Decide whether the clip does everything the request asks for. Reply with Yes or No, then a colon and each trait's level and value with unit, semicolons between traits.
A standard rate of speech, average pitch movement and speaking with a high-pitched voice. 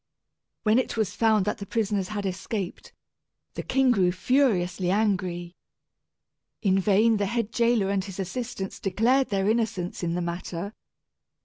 Yes: average, 145 wpm; average, 3.4 semitones; high, 200 Hz